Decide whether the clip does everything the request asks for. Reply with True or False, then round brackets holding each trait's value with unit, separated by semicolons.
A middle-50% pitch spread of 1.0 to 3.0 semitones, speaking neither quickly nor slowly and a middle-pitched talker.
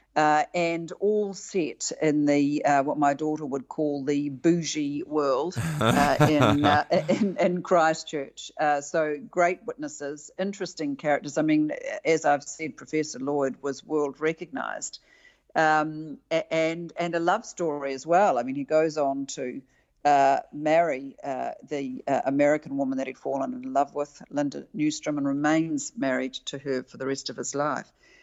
True (2.7 semitones; 160 wpm; 150 Hz)